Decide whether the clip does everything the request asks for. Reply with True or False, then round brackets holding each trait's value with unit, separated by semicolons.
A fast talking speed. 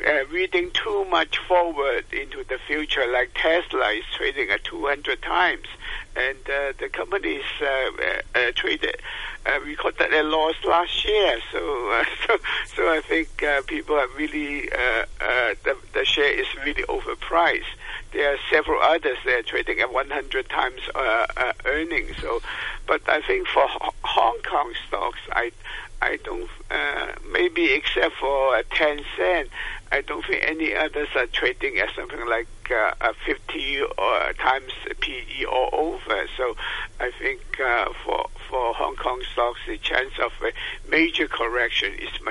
False (165 wpm)